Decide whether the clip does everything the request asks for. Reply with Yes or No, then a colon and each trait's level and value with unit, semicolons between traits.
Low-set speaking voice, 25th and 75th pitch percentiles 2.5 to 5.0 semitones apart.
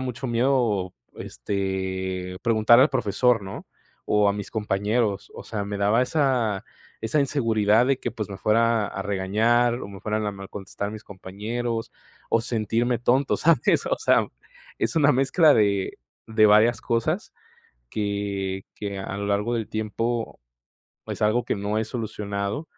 Yes: low, 110 Hz; average, 2.9 semitones